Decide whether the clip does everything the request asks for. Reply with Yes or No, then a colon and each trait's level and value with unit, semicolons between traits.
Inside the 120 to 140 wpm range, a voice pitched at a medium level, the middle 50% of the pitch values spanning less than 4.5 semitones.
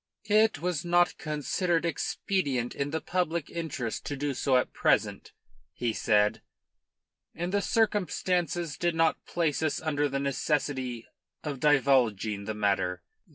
No: slow, 135 wpm; medium, 150 Hz; average, 5.2 semitones